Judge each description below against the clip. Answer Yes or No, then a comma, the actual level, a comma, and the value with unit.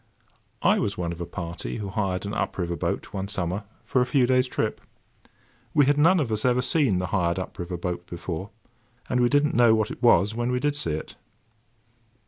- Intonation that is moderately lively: No, wide, 6.1 semitones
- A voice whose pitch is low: Yes, low, 105 Hz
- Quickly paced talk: Yes, fast, 220 wpm